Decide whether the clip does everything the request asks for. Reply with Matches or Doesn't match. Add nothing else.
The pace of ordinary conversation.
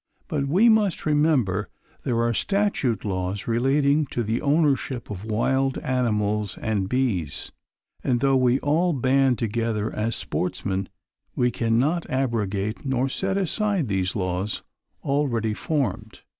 Doesn't match